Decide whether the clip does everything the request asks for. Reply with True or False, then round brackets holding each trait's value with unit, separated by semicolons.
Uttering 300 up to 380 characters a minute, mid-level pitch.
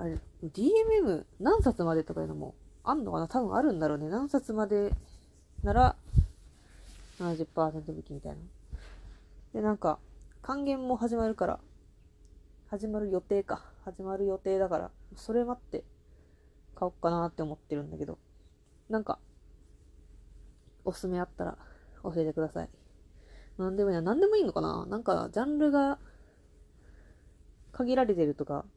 False (280 characters per minute; 160 Hz)